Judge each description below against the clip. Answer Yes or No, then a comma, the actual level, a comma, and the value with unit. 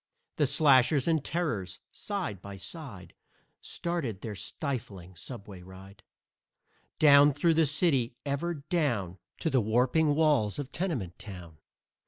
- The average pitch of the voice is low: Yes, low, 130 Hz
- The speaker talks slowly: Yes, slow, 125 wpm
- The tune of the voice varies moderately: No, wide, 7.9 semitones